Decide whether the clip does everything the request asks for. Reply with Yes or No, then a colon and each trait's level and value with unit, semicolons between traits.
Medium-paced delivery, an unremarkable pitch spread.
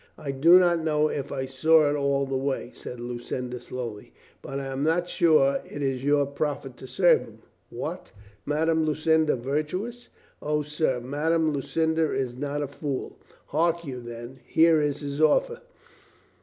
Yes: average, 170 wpm; average, 3.2 semitones